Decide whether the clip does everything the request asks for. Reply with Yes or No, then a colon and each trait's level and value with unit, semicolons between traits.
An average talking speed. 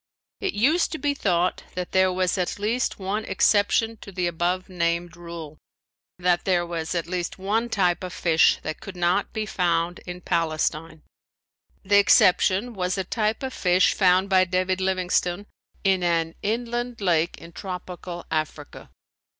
Yes: average, 160 wpm